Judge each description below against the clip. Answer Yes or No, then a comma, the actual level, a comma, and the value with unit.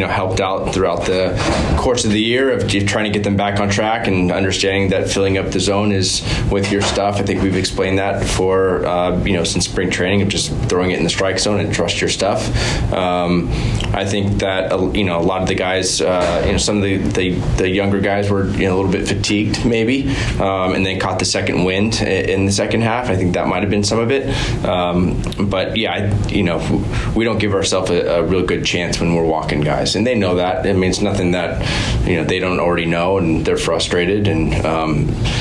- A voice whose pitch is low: Yes, very low, 95 Hz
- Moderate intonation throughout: No, narrow, 1.9 semitones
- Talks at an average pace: No, fast, 240 wpm